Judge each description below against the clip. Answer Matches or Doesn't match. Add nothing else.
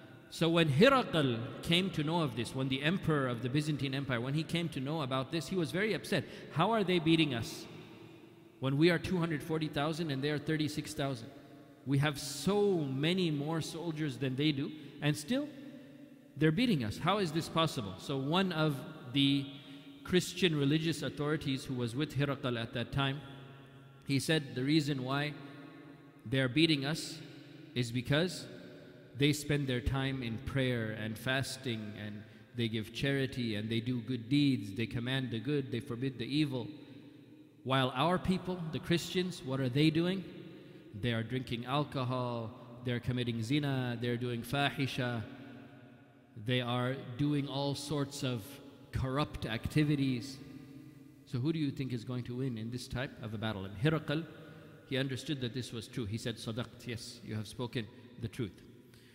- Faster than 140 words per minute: Matches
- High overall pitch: Doesn't match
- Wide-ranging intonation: Doesn't match